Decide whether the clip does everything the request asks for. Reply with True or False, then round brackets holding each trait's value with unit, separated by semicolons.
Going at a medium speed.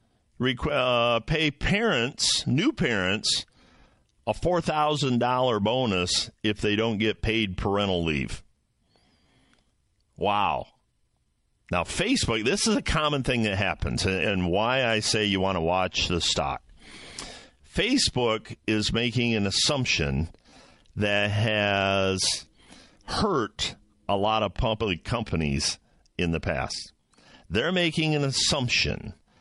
False (115 wpm)